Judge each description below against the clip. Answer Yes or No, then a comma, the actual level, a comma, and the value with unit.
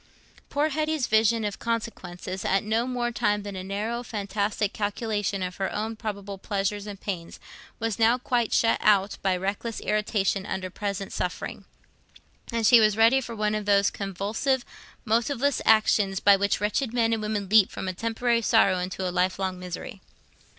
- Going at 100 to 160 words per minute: No, average, 170 wpm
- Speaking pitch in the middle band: No, high, 210 Hz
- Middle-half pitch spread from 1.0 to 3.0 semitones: Yes, average, 2.7 semitones